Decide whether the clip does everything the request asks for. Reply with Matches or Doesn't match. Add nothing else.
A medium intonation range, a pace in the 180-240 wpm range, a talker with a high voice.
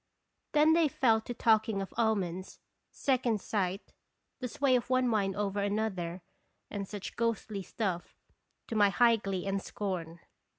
Doesn't match